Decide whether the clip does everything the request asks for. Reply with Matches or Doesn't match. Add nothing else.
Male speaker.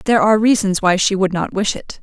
Doesn't match